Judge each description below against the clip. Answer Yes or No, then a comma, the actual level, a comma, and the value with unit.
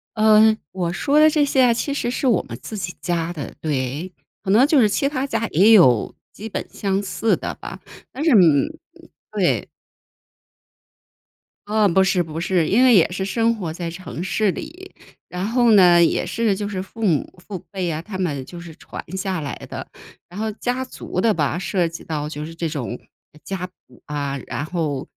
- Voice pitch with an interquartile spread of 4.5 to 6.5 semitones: Yes, average, 5.1 semitones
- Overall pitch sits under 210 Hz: Yes, high, 190 Hz